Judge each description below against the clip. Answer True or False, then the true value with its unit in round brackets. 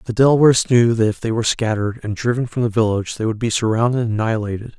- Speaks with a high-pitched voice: False (115 Hz)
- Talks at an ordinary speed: False (240 wpm)